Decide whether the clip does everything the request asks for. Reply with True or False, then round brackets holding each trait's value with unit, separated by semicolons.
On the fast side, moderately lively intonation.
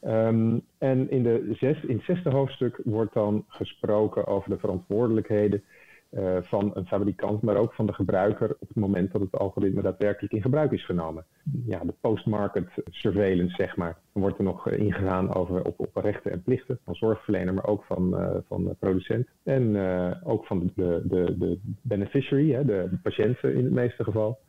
False (185 wpm; 3.3 semitones)